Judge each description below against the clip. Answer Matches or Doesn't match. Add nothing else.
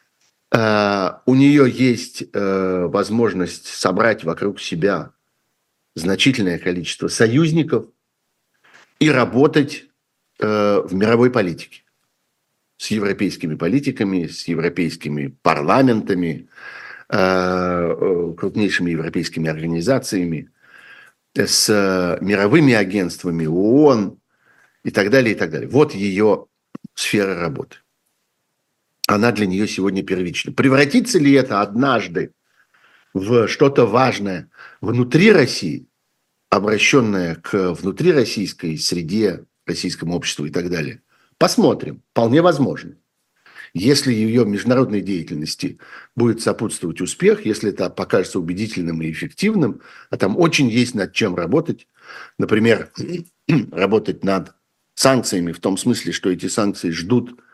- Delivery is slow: Matches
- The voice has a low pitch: Matches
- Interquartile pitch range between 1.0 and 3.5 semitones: Doesn't match